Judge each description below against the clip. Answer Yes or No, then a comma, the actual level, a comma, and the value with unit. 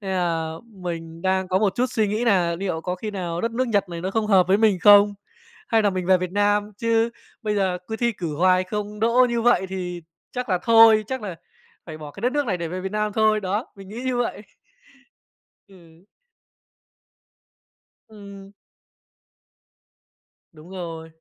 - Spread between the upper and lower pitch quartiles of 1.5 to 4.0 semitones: Yes, average, 3.3 semitones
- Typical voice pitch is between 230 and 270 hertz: No, high, 200 Hz